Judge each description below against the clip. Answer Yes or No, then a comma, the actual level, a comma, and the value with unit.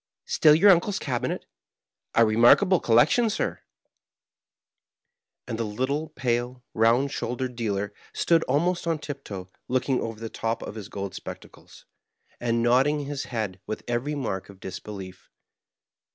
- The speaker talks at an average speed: Yes, average, 145 wpm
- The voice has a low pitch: Yes, low, 120 Hz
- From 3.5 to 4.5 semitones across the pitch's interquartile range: No, average, 4.9 semitones